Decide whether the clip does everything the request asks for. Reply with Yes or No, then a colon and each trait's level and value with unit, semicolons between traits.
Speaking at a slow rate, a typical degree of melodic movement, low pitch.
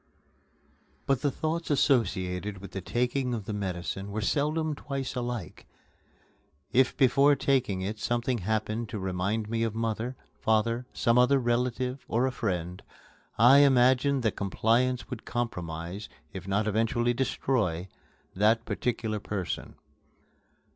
Yes: slow, 130 wpm; average, 3.8 semitones; low, 115 Hz